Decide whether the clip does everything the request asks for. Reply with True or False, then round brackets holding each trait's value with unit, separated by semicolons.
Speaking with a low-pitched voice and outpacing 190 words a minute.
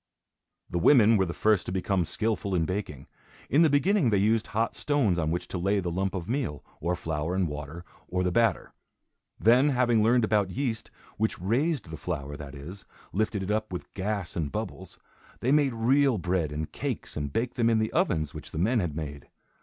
True (100 Hz; 205 wpm)